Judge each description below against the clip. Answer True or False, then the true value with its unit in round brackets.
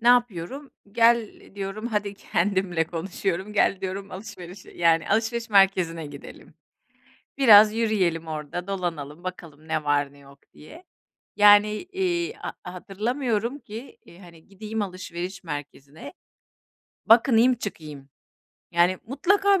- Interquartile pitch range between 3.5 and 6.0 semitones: True (5.0 semitones)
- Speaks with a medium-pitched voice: False (195 Hz)